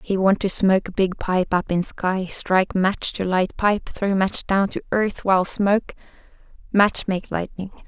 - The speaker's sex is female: Yes, female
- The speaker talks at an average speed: Yes, average, 175 wpm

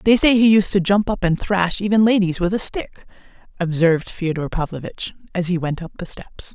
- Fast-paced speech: Yes, fast, 210 wpm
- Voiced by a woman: Yes, female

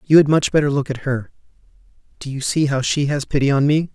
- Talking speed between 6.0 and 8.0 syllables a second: Yes, 6.1 syllables/s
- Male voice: Yes, male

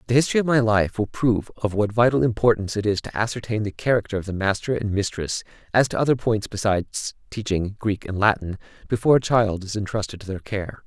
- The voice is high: No, low, 105 Hz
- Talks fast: Yes, fast, 215 wpm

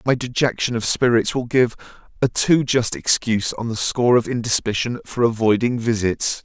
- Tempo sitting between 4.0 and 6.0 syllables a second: Yes, 5.3 syllables/s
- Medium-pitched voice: No, low, 115 Hz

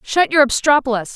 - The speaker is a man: No, female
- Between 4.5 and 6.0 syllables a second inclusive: Yes, 5.5 syllables/s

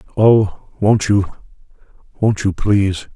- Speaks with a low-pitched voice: Yes, low, 100 Hz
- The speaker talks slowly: Yes, slow, 95 wpm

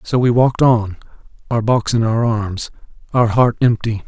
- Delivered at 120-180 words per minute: Yes, average, 175 wpm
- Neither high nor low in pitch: No, low, 115 Hz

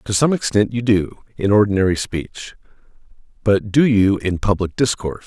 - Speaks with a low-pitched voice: Yes, low, 105 Hz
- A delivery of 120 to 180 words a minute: Yes, average, 160 wpm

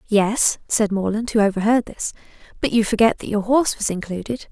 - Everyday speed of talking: Yes, average, 185 wpm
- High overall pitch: Yes, high, 215 Hz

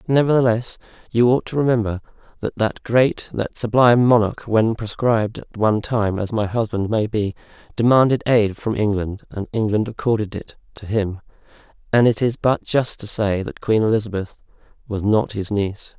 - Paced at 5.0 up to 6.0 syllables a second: Yes, 5.1 syllables/s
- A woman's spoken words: No, male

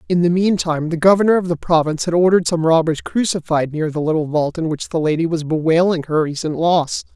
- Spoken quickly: Yes, fast, 220 wpm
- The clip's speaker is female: No, male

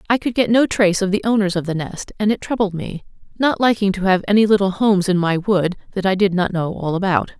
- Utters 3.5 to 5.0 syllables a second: No, 6.1 syllables/s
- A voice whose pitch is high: Yes, high, 195 Hz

